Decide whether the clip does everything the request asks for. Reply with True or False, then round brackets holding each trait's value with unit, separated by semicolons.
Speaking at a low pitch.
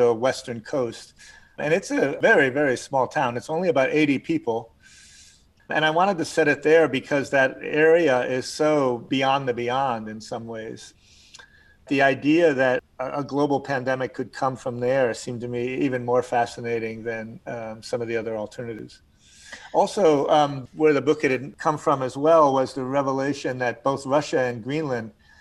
True (130 Hz)